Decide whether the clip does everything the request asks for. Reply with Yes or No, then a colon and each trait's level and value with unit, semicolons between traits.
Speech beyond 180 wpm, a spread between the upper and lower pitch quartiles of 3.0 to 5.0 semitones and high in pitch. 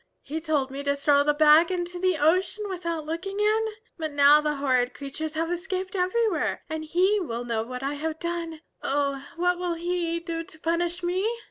Yes: average, 195 wpm; average, 3.6 semitones; very high, 330 Hz